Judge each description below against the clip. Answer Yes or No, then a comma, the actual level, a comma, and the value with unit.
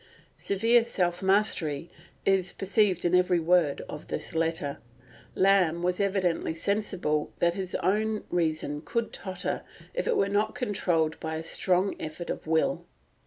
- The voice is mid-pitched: Yes, medium, 180 Hz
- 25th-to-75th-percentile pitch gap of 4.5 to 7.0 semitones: No, average, 3.6 semitones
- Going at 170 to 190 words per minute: No, average, 145 wpm